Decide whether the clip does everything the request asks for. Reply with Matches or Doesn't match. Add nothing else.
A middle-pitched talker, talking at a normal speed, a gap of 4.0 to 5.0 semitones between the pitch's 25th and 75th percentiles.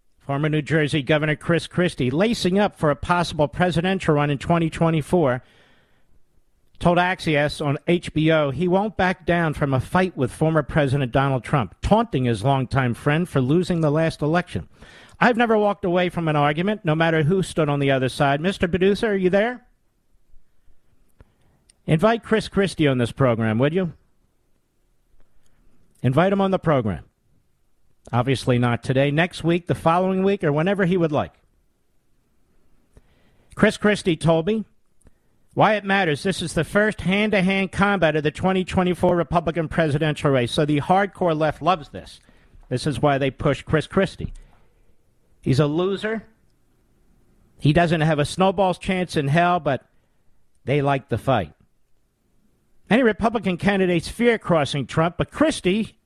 Matches